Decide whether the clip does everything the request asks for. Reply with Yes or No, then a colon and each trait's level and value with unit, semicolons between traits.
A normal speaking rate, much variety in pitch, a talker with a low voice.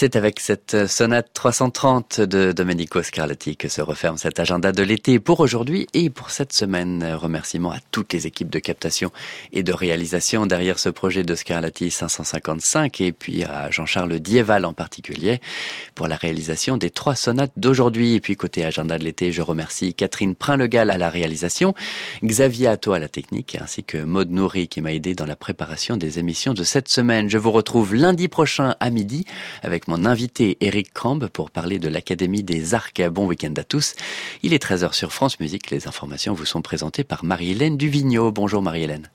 Yes: average, 190 wpm; wide, 6.1 semitones; very low, 95 Hz